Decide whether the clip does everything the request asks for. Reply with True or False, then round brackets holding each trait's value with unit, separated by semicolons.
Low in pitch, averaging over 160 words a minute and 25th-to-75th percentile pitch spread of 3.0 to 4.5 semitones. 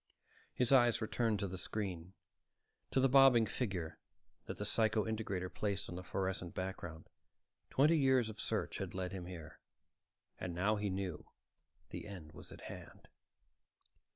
False (100 Hz; 155 wpm; 3.8 semitones)